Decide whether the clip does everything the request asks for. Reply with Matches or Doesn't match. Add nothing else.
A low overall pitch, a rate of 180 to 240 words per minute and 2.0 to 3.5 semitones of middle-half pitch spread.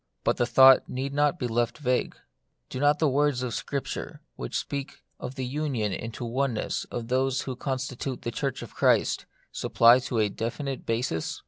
Matches